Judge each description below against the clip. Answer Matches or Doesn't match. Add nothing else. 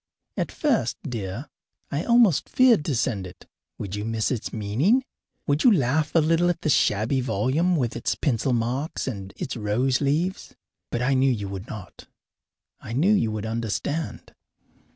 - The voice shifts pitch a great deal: Matches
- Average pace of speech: Matches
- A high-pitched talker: Doesn't match